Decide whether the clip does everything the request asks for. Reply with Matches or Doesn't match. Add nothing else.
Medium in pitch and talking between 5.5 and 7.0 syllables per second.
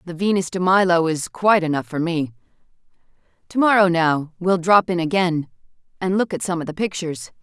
Matches